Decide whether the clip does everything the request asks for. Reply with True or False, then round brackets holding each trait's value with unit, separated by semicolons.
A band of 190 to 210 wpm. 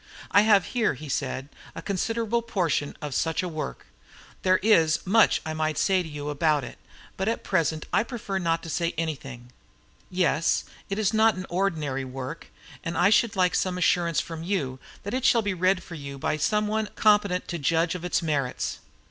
True (195 wpm)